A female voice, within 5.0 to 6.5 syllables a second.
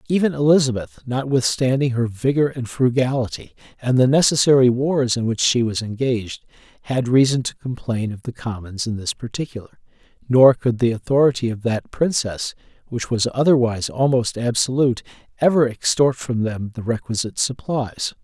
No: male; 5.2 syllables/s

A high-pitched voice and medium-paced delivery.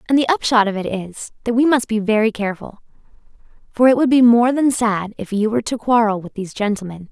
No: high, 225 Hz; fast, 230 wpm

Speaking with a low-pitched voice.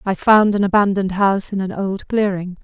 No: high, 195 Hz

